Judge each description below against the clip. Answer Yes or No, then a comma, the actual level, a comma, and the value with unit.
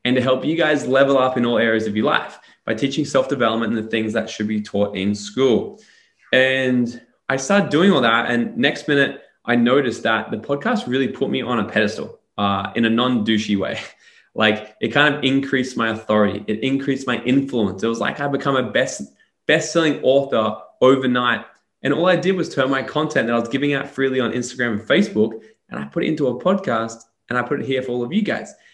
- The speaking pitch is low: Yes, low, 125 Hz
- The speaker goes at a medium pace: No, fast, 220 wpm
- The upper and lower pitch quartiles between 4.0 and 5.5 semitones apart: No, average, 3.5 semitones